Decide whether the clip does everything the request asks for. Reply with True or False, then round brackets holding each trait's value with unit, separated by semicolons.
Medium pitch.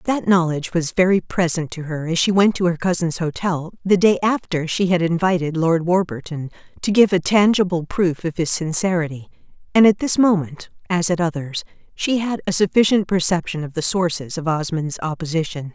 True (175 Hz)